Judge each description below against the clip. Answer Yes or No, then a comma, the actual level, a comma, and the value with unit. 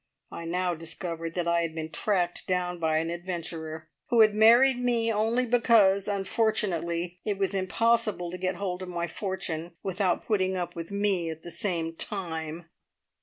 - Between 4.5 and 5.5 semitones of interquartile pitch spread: No, average, 3.6 semitones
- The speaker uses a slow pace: No, average, 170 wpm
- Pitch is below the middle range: No, medium, 180 Hz